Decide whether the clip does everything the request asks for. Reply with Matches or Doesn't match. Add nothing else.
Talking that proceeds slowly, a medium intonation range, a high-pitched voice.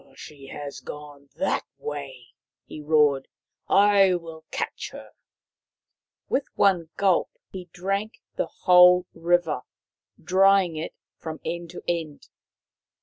Doesn't match